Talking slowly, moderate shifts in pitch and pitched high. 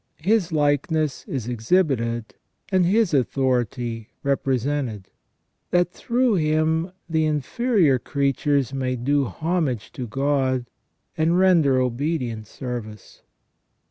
No: slow, 100 wpm; average, 4.6 semitones; medium, 140 Hz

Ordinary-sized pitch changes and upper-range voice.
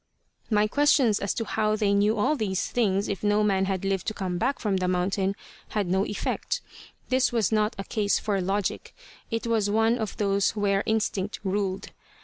No: narrow, 2.0 semitones; high, 205 Hz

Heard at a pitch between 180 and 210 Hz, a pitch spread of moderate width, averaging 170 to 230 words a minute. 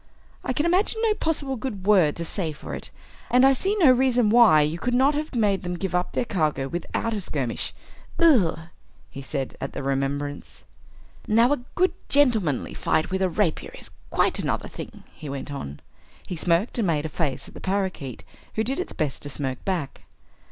No: high, 190 Hz; wide, 8.8 semitones; average, 195 wpm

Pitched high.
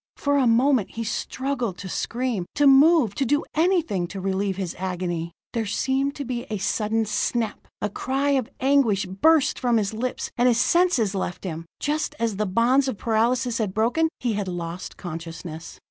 Yes: high, 230 Hz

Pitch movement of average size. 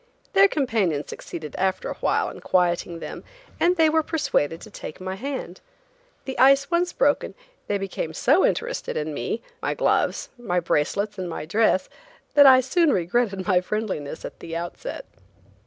No: wide, 8.3 semitones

